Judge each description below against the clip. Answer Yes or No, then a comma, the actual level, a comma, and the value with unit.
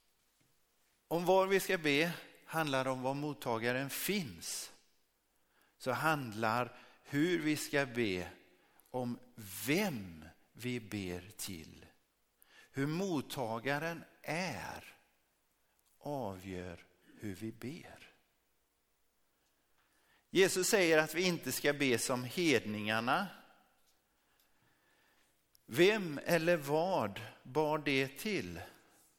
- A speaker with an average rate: No, slow, 90 wpm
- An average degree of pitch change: No, wide, 6.1 semitones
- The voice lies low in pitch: Yes, low, 130 Hz